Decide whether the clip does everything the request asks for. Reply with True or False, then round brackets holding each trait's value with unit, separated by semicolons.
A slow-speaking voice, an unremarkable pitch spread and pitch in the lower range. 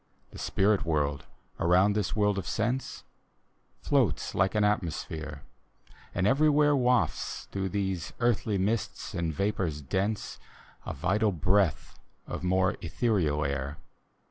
True (120 wpm; 4.5 semitones; 95 Hz)